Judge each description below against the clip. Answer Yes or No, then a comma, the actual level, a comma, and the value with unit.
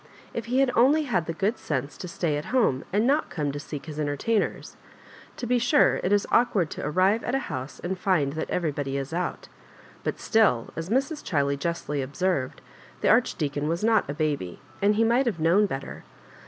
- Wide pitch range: Yes, wide, 7.7 semitones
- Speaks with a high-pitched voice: No, medium, 175 Hz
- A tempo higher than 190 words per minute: Yes, average, 200 wpm